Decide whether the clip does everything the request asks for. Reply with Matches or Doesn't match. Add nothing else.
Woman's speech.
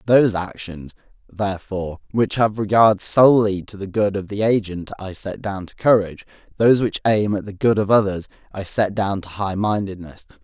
Doesn't match